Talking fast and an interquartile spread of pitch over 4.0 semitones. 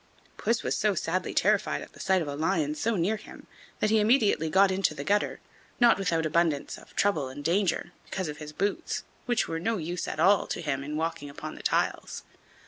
Yes: fast, 220 wpm; average, 4.8 semitones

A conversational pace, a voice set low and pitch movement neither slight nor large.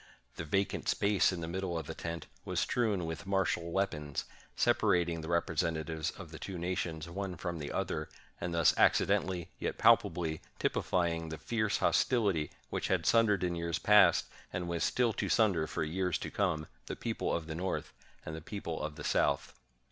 Yes: average, 180 wpm; very low, 85 Hz; average, 3.0 semitones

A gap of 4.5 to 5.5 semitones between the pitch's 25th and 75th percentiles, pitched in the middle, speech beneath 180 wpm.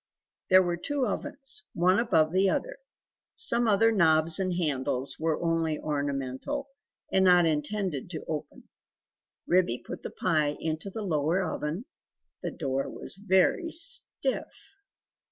Yes: average, 4.8 semitones; medium, 175 Hz; slow, 135 wpm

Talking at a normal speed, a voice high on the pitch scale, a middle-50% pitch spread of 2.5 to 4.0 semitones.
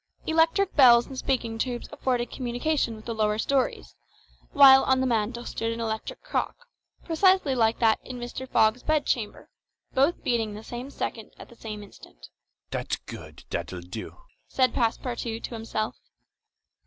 Yes: average, 155 wpm; high, 240 Hz; average, 3.1 semitones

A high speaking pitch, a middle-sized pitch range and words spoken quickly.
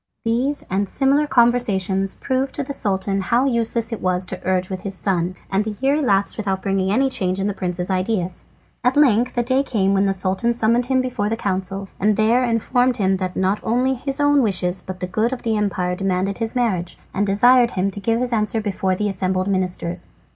Yes: high, 205 Hz; average, 4.2 semitones; fast, 210 wpm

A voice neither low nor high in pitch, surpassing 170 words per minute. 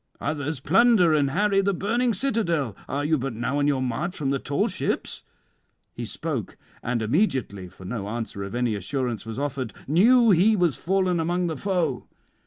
Yes: medium, 145 Hz; average, 180 wpm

